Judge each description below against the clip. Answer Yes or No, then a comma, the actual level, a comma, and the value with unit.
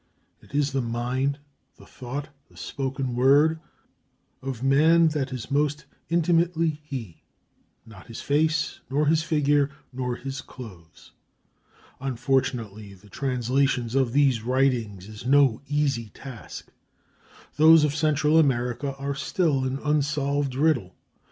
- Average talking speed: No, slow, 125 wpm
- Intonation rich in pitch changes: No, average, 3.3 semitones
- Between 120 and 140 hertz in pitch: Yes, low, 135 Hz